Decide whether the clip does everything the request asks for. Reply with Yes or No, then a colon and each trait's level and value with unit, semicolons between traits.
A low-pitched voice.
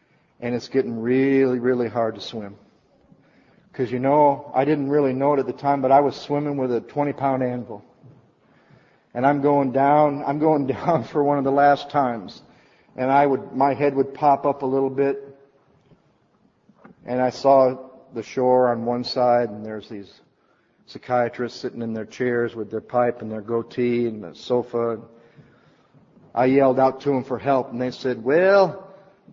Yes: low, 130 Hz